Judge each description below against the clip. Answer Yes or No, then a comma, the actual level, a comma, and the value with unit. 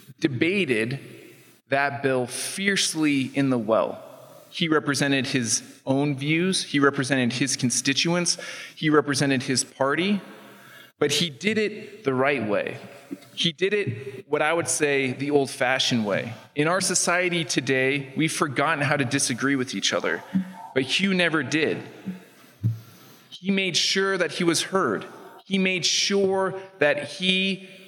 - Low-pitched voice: No, medium, 145 Hz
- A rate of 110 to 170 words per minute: Yes, average, 140 wpm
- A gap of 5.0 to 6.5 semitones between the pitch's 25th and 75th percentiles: Yes, wide, 5.5 semitones